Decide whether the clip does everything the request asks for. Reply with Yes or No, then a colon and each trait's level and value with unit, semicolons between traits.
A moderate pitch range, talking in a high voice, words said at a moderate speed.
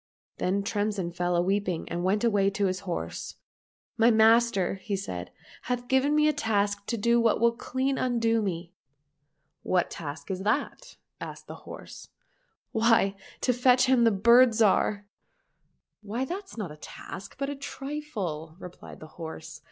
Yes: average, 4.8 semitones; high, 210 Hz; average, 185 wpm